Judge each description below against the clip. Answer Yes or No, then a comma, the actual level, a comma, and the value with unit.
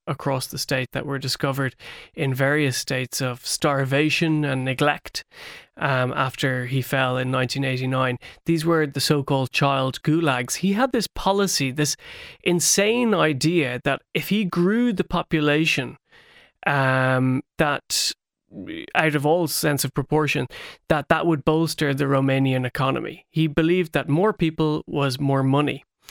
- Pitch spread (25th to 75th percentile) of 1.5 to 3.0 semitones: No, average, 3.5 semitones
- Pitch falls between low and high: Yes, medium, 145 Hz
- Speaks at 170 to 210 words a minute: No, average, 140 wpm